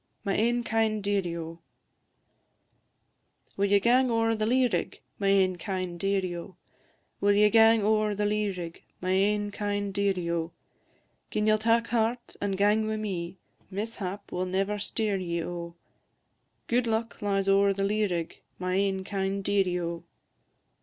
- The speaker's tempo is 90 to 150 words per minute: No, average, 160 wpm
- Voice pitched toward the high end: Yes, high, 200 Hz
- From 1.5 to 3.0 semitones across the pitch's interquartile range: Yes, narrow, 2.6 semitones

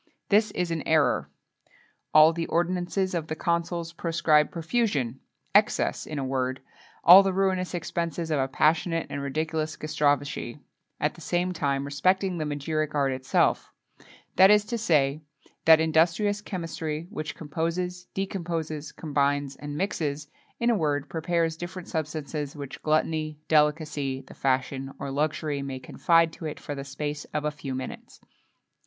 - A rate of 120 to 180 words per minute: Yes, average, 150 wpm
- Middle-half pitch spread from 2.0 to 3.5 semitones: Yes, average, 2.9 semitones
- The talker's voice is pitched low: No, medium, 155 Hz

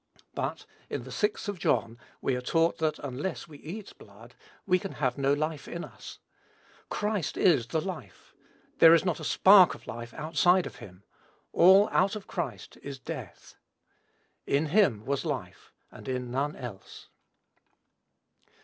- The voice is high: No, medium, 155 Hz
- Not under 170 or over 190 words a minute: No, average, 155 wpm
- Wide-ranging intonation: Yes, wide, 6.5 semitones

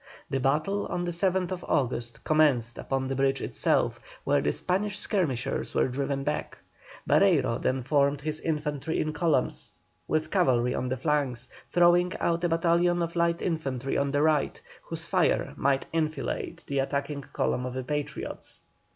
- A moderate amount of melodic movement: Yes, average, 4.0 semitones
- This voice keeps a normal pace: Yes, average, 160 wpm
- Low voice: No, medium, 150 Hz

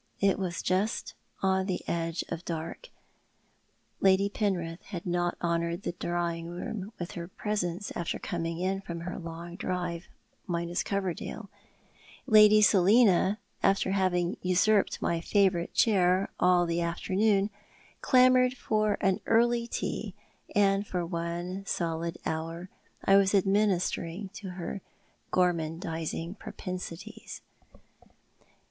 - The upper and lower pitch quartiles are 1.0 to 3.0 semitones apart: Yes, average, 2.7 semitones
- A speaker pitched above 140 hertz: Yes, medium, 185 Hz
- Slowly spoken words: Yes, slow, 115 wpm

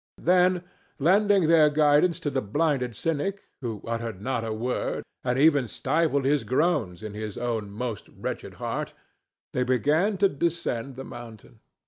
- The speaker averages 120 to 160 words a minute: Yes, average, 150 wpm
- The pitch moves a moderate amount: No, wide, 5.9 semitones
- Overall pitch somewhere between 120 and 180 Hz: Yes, low, 135 Hz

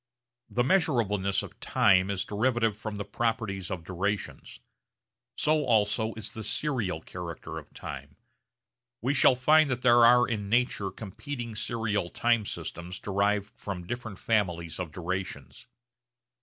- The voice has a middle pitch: No, low, 105 Hz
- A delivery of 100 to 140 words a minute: Yes, slow, 135 wpm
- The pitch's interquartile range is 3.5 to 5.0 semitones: Yes, average, 4.0 semitones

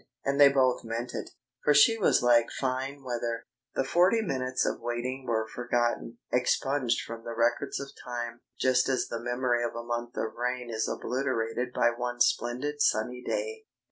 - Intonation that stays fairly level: Yes, narrow, 2.1 semitones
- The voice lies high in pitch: No, low, 125 Hz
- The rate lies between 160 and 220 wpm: Yes, average, 175 wpm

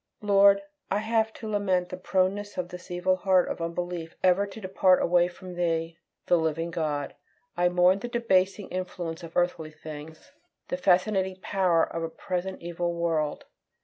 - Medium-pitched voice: Yes, medium, 180 Hz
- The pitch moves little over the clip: Yes, narrow, 2.3 semitones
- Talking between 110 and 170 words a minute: Yes, average, 165 wpm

